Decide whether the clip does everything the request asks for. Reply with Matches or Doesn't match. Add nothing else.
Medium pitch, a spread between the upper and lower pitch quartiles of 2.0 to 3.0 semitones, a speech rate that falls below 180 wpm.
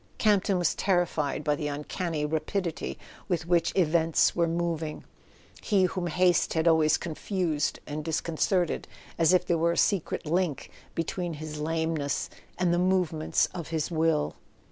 Matches